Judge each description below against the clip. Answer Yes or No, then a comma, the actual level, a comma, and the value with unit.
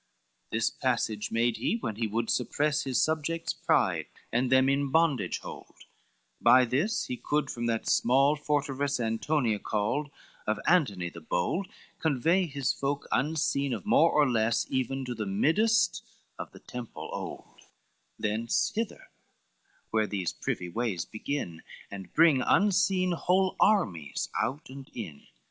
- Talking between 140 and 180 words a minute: Yes, average, 145 wpm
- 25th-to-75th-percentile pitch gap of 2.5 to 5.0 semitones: No, wide, 5.4 semitones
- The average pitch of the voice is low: Yes, low, 130 Hz